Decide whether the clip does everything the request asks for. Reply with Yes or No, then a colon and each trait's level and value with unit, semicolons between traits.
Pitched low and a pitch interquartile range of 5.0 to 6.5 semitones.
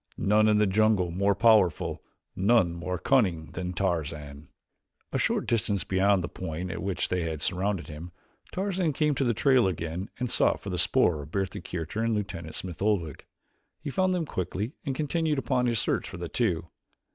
Yes: very low, 95 Hz; wide, 5.4 semitones